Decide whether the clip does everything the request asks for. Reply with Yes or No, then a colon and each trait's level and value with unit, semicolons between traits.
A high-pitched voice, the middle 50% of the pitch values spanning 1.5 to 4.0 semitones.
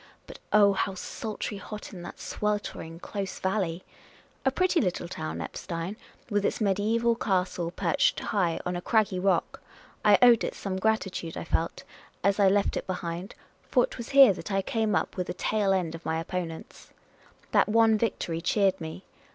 Yes: high, 195 Hz; average, 3.3 semitones